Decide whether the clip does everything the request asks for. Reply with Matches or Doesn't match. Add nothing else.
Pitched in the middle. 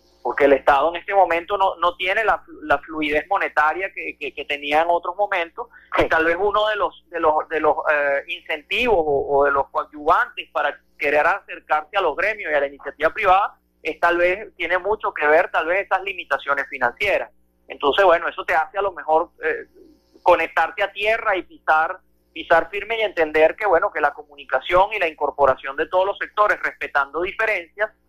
Matches